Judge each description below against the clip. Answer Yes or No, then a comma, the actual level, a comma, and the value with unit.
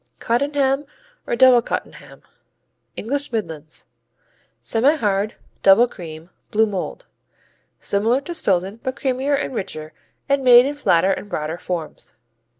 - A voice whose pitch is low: No, high, 230 Hz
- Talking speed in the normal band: No, slow, 120 wpm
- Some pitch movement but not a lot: No, wide, 6.0 semitones